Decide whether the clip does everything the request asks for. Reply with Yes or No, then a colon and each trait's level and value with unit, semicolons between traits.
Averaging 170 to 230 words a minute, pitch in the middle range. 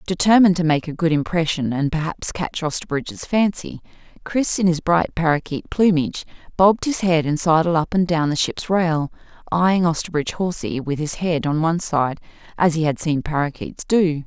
Yes: average, 180 wpm; medium, 165 Hz